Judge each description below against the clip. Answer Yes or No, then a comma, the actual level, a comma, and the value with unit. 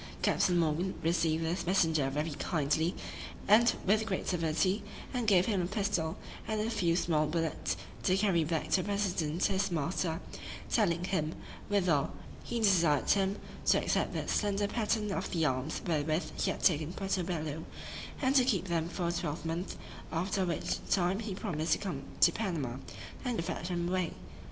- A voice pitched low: No, medium, 175 Hz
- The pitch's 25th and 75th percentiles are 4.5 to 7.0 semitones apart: No, average, 3.5 semitones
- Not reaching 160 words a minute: No, average, 165 wpm